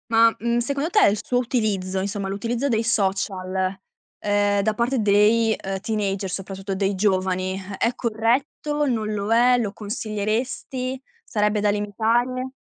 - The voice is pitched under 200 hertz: No, high, 215 Hz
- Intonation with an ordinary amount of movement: Yes, average, 3.2 semitones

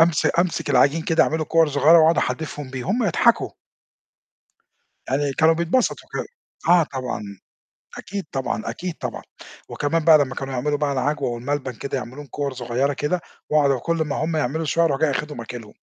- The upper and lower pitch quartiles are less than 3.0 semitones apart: No, average, 3.3 semitones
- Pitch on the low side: No, medium, 145 Hz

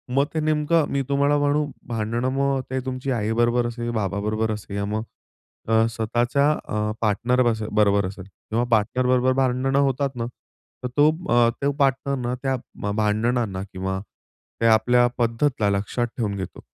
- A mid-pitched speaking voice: No, low, 120 Hz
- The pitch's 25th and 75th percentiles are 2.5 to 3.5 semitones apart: No, average, 3.9 semitones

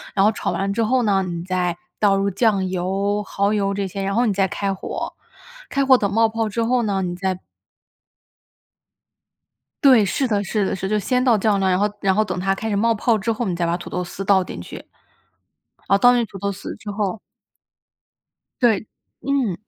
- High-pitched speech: Yes, high, 200 Hz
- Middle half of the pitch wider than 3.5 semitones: No, average, 2.7 semitones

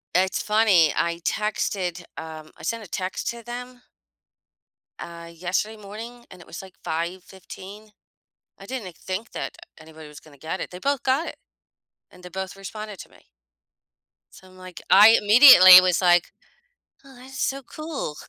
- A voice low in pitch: No, high, 190 Hz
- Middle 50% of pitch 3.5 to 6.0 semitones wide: Yes, average, 4.2 semitones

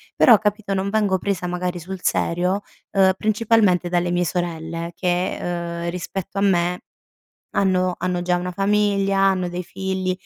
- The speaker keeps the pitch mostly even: Yes, narrow, 1.9 semitones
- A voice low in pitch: No, medium, 185 Hz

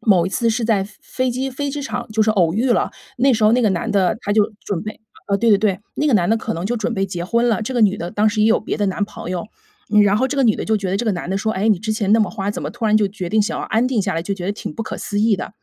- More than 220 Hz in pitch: No, high, 215 Hz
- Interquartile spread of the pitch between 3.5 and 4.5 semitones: No, average, 2.8 semitones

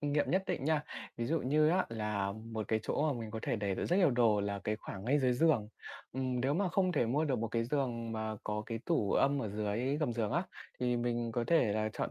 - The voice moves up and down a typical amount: Yes, average, 4.9 semitones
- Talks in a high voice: No, low, 120 Hz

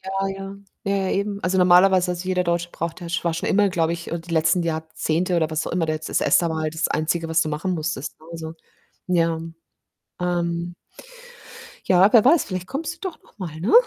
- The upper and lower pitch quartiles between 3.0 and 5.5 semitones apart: No, narrow, 2.5 semitones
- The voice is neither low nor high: Yes, medium, 175 Hz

